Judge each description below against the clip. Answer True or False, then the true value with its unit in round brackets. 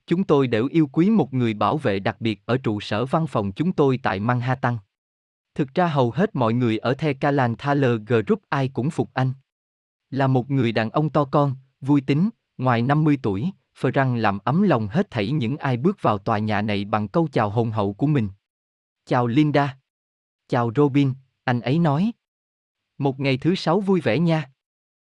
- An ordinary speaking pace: True (195 wpm)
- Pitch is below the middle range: True (130 Hz)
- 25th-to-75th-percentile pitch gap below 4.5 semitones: False (5.1 semitones)